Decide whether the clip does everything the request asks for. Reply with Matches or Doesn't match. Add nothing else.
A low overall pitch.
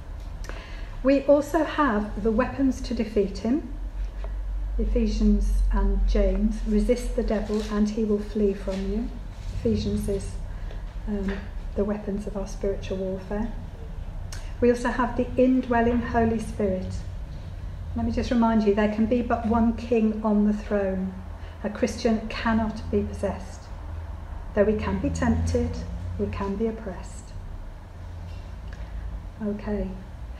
Doesn't match